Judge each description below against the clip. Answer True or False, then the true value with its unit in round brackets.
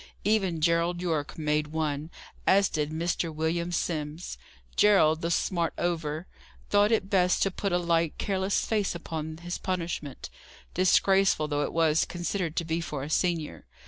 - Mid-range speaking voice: True (170 Hz)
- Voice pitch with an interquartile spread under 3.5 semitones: True (2.7 semitones)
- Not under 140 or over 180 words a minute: True (155 wpm)